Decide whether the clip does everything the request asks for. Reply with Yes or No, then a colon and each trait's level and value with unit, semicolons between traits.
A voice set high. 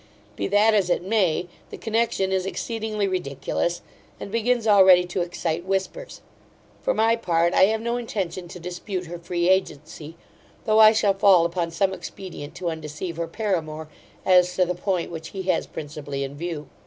No: medium, 180 Hz